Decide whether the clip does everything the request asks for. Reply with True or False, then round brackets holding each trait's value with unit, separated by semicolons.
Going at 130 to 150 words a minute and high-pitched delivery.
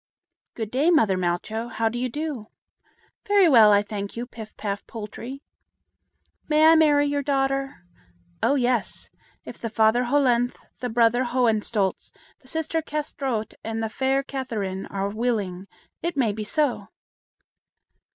True (140 wpm; 240 Hz)